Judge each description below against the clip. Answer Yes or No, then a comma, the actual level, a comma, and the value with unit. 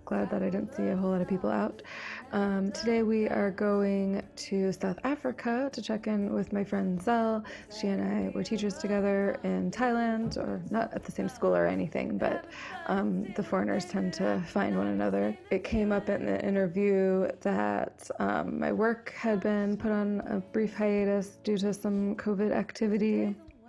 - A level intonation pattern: Yes, narrow, 2.0 semitones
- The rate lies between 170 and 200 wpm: Yes, average, 185 wpm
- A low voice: No, high, 200 Hz